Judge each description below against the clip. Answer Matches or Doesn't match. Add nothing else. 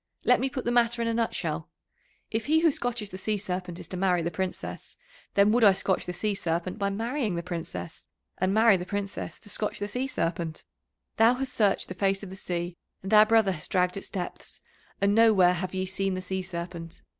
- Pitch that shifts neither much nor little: Matches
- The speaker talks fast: Matches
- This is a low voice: Doesn't match